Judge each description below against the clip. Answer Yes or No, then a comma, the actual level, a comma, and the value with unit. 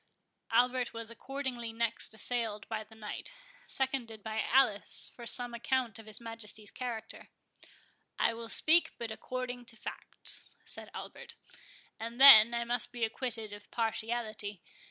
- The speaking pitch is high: Yes, high, 230 Hz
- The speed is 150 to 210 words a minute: No, average, 140 wpm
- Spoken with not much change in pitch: Yes, narrow, 2.0 semitones